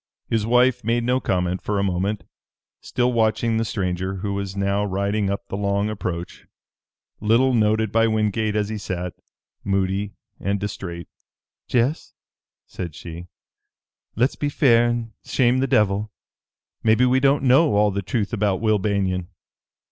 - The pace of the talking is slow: No, average, 150 wpm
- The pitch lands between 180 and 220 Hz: No, low, 105 Hz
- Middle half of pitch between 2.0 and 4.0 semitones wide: Yes, average, 3.0 semitones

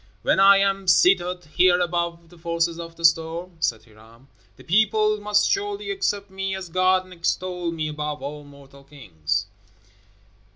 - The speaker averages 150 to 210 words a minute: Yes, average, 160 wpm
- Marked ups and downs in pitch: No, average, 4.1 semitones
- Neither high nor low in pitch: Yes, medium, 170 Hz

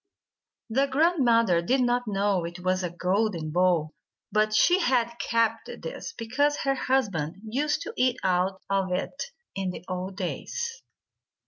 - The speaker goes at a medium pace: Yes, average, 145 wpm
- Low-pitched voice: No, high, 215 Hz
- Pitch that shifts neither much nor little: No, wide, 6.2 semitones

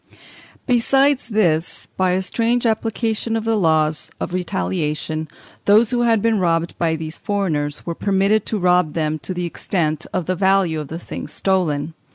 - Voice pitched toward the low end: No, medium, 185 Hz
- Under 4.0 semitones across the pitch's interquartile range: No, wide, 5.4 semitones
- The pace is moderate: Yes, average, 170 wpm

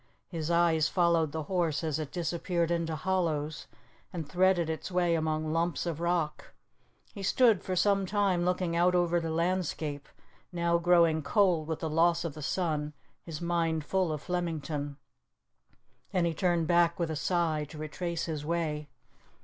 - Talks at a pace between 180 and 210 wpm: No, average, 165 wpm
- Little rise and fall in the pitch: Yes, narrow, 2.1 semitones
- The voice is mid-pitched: Yes, medium, 170 Hz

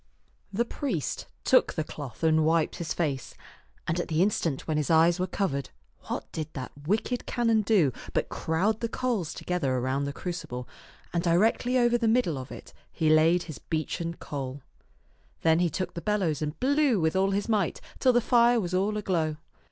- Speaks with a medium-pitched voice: Yes, medium, 170 Hz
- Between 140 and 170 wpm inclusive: No, average, 185 wpm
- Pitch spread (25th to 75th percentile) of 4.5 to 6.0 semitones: Yes, average, 5.3 semitones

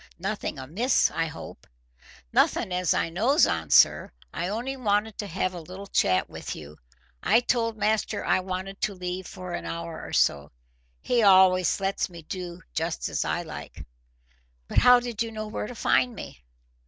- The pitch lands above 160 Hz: Yes, high, 190 Hz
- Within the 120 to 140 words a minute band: No, average, 180 wpm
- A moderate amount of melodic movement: Yes, average, 4.0 semitones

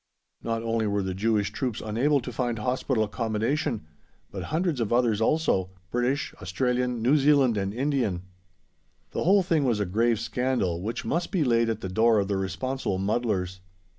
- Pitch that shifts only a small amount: No, average, 3.9 semitones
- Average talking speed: Yes, average, 170 wpm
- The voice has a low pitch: Yes, low, 115 Hz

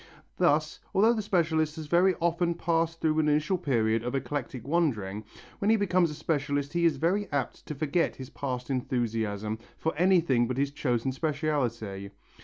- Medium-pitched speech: Yes, medium, 150 Hz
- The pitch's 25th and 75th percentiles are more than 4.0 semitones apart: Yes, average, 5.1 semitones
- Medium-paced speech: Yes, average, 170 wpm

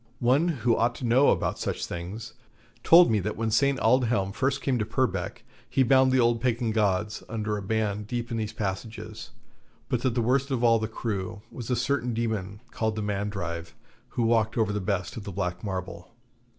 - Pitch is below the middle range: Yes, low, 110 Hz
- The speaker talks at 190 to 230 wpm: Yes, average, 200 wpm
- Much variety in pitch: No, average, 3.0 semitones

